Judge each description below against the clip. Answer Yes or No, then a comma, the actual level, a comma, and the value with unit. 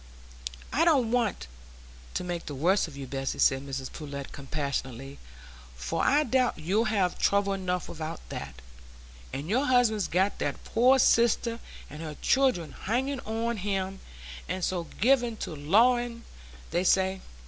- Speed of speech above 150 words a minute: No, average, 145 wpm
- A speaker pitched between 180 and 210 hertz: Yes, high, 190 Hz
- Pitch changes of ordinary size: No, wide, 7.7 semitones